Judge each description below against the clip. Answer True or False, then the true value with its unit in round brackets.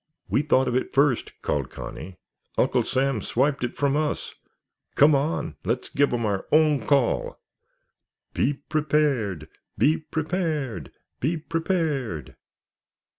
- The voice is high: False (140 Hz)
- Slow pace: True (125 wpm)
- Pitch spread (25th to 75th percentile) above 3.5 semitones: True (4.3 semitones)